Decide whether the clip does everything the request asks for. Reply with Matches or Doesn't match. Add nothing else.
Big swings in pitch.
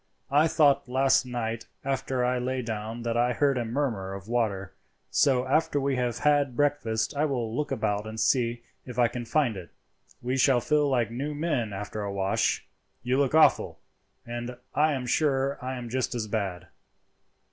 Doesn't match